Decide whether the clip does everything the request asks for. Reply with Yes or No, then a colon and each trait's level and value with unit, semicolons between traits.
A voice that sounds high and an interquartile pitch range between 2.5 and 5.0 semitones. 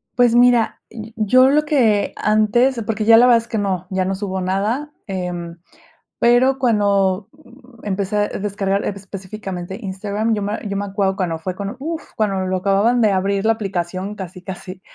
Yes: high, 205 Hz; average, 3.4 semitones